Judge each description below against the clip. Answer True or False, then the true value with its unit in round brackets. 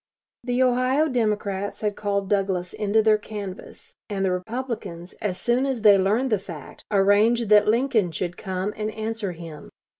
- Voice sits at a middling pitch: False (210 Hz)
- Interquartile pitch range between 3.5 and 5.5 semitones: False (3.1 semitones)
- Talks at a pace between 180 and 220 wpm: False (160 wpm)